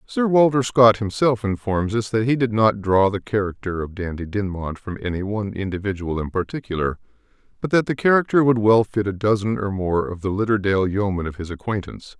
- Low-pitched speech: Yes, low, 105 Hz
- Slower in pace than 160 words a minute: No, average, 195 wpm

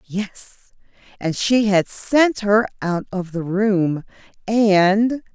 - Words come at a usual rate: No, slow, 125 wpm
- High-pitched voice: Yes, high, 205 Hz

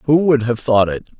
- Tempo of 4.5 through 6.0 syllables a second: Yes, 5.3 syllables/s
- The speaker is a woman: No, male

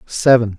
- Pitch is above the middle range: No, low, 115 Hz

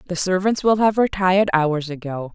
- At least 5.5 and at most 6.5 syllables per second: No, 5.2 syllables/s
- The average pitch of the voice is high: No, medium, 180 Hz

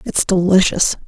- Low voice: No, medium, 185 Hz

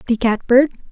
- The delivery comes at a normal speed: Yes, average, 195 wpm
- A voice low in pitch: No, high, 245 Hz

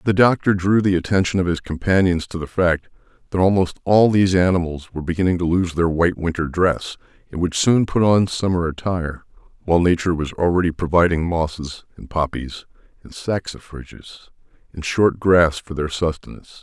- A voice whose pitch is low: Yes, very low, 90 Hz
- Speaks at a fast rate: No, average, 170 wpm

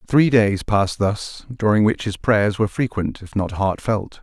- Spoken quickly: No, average, 185 wpm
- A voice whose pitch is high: No, low, 105 Hz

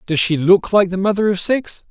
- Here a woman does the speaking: No, male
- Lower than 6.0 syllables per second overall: Yes, 5.1 syllables/s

